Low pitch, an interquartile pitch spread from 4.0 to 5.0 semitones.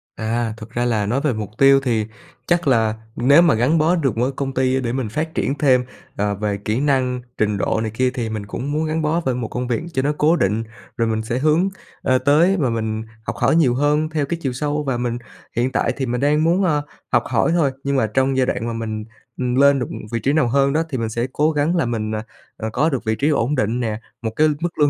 Yes: low, 130 Hz; average, 4.5 semitones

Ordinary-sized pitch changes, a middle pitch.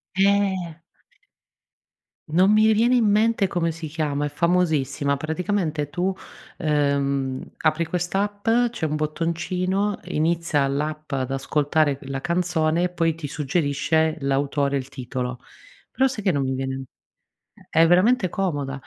Yes: average, 4.3 semitones; medium, 160 Hz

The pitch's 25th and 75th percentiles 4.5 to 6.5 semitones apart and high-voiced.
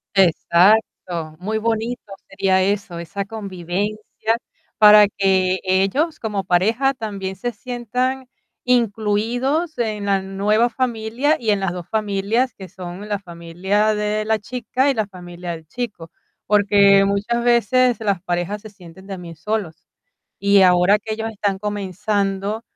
No: average, 2.8 semitones; high, 205 Hz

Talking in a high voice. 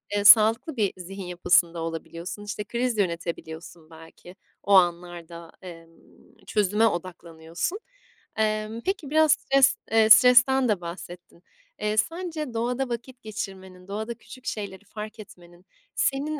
Yes: high, 205 Hz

